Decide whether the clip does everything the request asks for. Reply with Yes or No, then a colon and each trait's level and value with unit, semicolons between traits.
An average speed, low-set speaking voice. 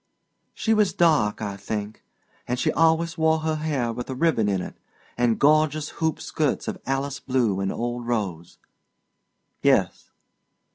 Yes: average, 150 wpm; low, 130 Hz